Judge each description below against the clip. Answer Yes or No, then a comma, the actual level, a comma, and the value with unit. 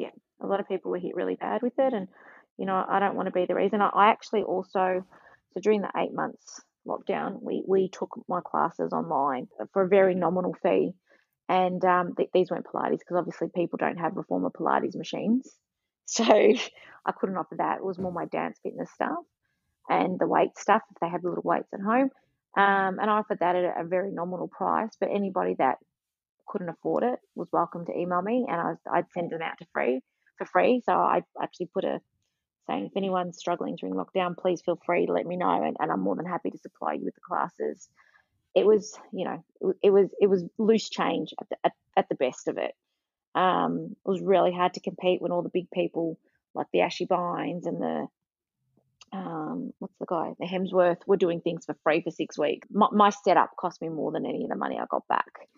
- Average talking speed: No, fast, 225 wpm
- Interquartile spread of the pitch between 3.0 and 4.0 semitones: No, narrow, 2.6 semitones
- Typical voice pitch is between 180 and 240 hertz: Yes, medium, 185 Hz